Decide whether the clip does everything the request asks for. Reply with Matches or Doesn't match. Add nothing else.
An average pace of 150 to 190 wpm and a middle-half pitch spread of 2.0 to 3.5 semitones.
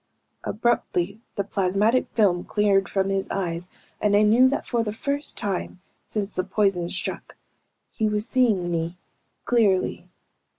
Doesn't match